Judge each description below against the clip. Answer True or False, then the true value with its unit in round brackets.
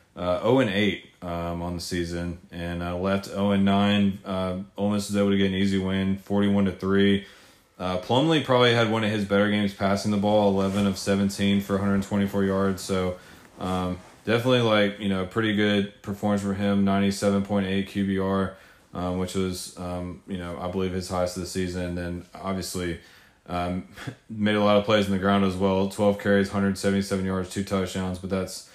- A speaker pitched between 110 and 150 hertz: False (100 Hz)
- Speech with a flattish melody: True (1.6 semitones)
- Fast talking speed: True (210 wpm)